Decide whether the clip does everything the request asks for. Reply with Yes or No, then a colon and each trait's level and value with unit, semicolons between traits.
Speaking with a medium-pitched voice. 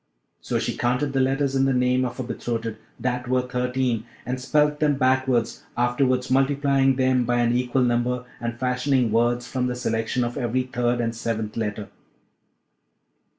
No: low, 125 Hz